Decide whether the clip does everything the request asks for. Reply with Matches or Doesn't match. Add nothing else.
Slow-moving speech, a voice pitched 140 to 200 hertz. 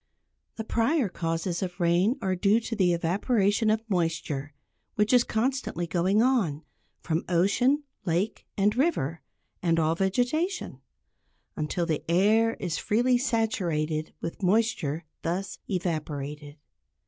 Matches